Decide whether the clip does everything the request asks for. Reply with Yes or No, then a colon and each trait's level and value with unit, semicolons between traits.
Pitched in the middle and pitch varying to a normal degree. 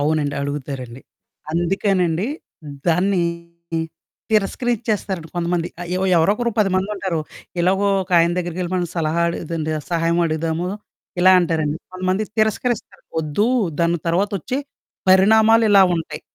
Yes: medium, 175 Hz; average, 3.2 semitones